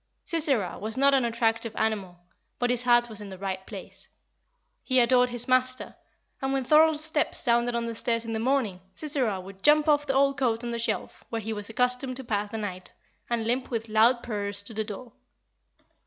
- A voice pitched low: No, high, 235 Hz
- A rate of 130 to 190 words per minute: No, fast, 205 wpm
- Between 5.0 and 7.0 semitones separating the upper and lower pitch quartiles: No, average, 3.1 semitones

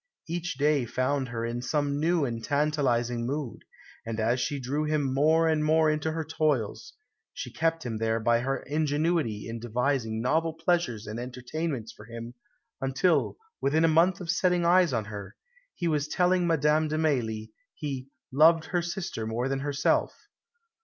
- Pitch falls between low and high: Yes, medium, 145 Hz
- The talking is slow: No, average, 165 wpm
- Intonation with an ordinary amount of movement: Yes, average, 5.0 semitones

